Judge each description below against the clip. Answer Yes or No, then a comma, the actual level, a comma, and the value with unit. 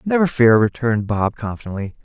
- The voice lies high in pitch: No, low, 120 Hz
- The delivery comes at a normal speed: Yes, average, 145 wpm